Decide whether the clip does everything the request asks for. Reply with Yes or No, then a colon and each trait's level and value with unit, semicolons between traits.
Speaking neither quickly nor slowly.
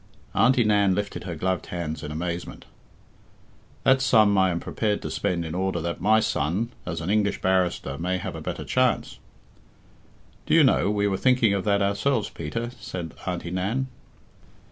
Yes: average, 175 wpm